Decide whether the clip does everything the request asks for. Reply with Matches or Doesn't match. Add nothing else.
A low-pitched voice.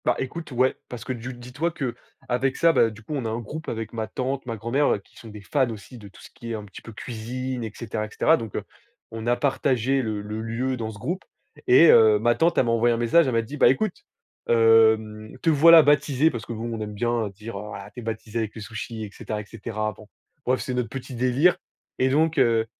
Matches